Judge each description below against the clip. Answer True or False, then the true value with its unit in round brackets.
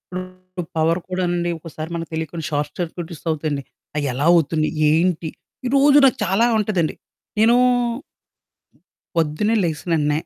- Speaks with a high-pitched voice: False (170 Hz)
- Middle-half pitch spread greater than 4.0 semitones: False (2.9 semitones)